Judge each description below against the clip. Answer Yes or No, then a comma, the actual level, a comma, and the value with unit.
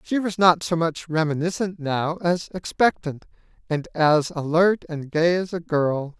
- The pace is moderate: Yes, average, 165 wpm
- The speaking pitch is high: No, medium, 165 Hz